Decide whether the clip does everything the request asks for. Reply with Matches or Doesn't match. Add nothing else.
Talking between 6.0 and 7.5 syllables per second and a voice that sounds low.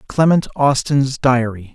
Doesn't match